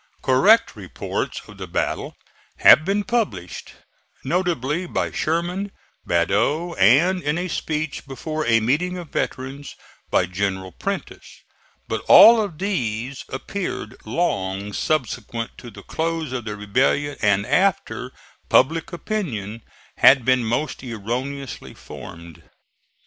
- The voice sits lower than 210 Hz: Yes, low, 135 Hz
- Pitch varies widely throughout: Yes, wide, 7.9 semitones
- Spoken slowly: Yes, slow, 120 wpm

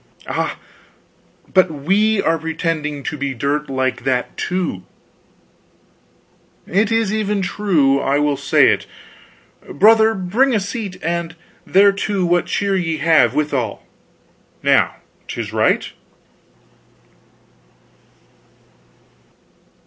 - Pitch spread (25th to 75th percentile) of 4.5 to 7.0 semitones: Yes, wide, 5.6 semitones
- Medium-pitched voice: Yes, medium, 170 Hz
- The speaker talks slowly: Yes, slow, 100 wpm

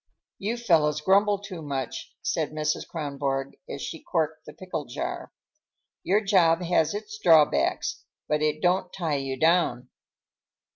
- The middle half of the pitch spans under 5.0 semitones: Yes, average, 4.3 semitones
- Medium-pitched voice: Yes, medium, 165 Hz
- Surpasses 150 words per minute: No, average, 140 wpm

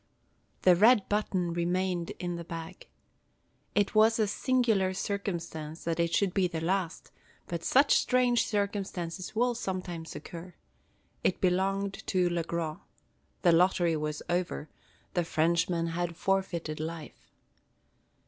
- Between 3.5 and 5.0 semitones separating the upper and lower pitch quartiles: No, average, 2.9 semitones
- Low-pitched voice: No, medium, 180 Hz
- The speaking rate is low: Yes, slow, 130 wpm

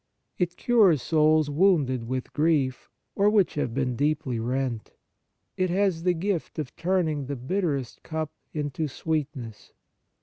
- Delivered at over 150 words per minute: No, slow, 135 wpm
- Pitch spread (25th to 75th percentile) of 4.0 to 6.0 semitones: Yes, average, 5.1 semitones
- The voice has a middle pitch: Yes, medium, 155 Hz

